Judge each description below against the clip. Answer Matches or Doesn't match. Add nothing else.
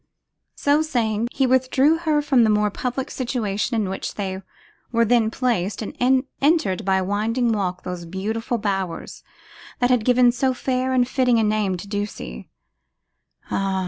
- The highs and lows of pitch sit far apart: Doesn't match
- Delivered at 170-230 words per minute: Doesn't match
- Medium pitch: Doesn't match